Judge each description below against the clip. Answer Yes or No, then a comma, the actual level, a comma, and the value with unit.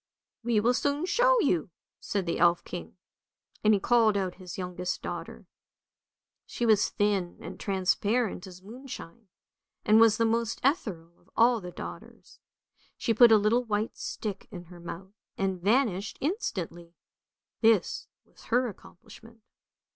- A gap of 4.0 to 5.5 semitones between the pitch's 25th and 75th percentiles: Yes, average, 4.3 semitones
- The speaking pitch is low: No, high, 210 Hz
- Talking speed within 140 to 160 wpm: Yes, average, 155 wpm